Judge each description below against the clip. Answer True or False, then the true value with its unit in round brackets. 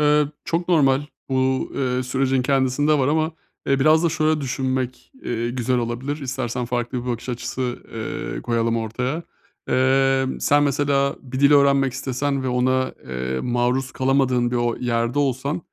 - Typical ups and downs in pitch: False (2.3 semitones)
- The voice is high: False (130 Hz)